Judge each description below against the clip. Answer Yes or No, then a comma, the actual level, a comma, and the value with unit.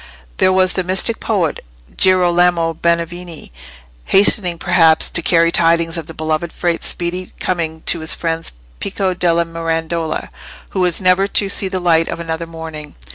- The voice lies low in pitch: No, medium, 170 Hz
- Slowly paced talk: No, average, 155 wpm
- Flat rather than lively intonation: Yes, narrow, 1.9 semitones